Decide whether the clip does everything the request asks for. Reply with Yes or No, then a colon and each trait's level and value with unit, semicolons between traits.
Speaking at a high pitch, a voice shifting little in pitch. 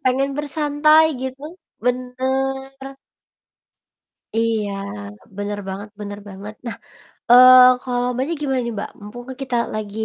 No: very high, 250 Hz; average, 3.8 semitones